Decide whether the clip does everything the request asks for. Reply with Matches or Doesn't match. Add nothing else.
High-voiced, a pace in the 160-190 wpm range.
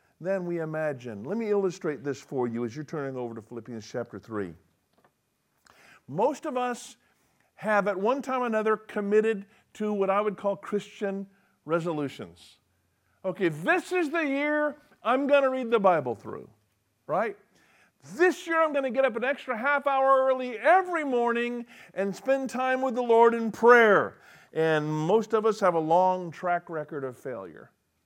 Matches